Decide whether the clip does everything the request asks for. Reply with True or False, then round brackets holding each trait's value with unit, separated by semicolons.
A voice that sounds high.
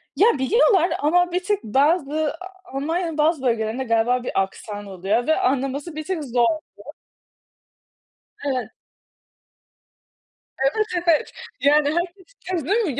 True (295 Hz)